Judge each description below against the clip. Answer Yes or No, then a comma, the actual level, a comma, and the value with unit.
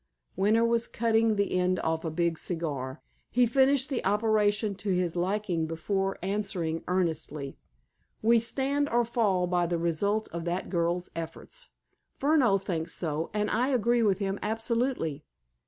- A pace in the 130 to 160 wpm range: Yes, average, 150 wpm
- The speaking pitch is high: Yes, high, 195 Hz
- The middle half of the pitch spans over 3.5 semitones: Yes, average, 5.2 semitones